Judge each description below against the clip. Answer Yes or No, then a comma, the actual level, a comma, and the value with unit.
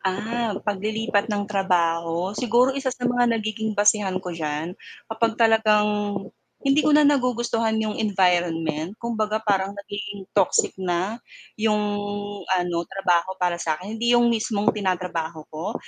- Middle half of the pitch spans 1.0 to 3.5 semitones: No, average, 3.9 semitones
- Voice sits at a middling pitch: No, high, 210 Hz